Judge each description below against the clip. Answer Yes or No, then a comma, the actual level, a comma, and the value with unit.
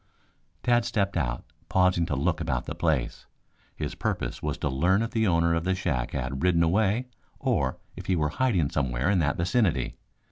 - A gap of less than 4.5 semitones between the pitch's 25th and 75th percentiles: No, average, 5.2 semitones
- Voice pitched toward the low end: Yes, very low, 85 Hz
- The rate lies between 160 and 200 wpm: Yes, average, 185 wpm